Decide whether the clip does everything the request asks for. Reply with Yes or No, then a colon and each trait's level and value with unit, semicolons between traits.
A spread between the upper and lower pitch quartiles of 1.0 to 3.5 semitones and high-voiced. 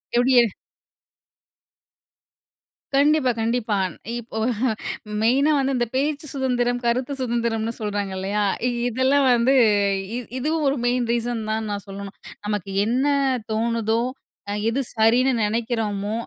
Yes: average, 3.0 semitones; high, 235 Hz